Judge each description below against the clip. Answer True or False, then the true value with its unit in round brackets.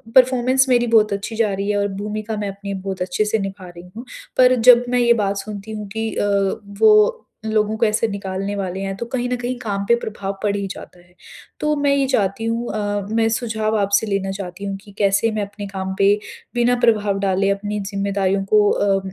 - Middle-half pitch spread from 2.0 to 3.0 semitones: True (2.4 semitones)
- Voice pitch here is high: True (205 Hz)